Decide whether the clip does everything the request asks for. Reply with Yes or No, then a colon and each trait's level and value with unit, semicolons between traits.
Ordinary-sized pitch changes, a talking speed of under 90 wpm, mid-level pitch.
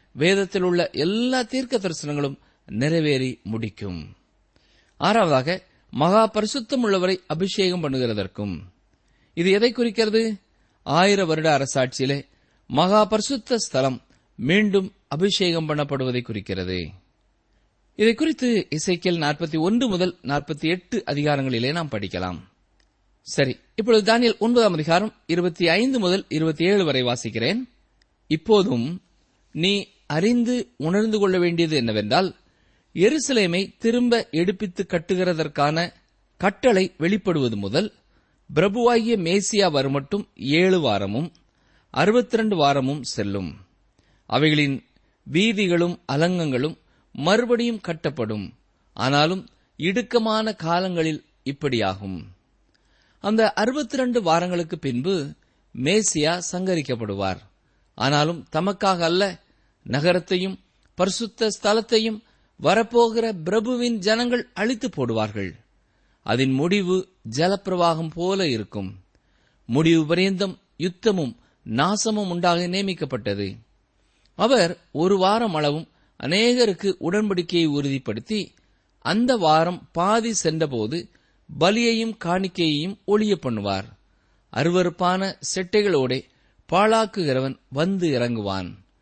No: wide, 7.6 semitones; average, 80 wpm; medium, 175 Hz